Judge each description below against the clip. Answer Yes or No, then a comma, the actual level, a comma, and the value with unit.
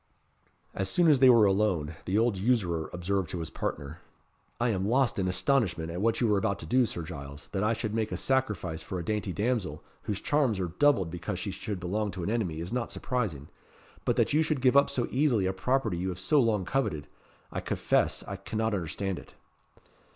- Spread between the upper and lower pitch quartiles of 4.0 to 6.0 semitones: Yes, average, 5.2 semitones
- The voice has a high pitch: No, low, 100 Hz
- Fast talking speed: Yes, fast, 215 wpm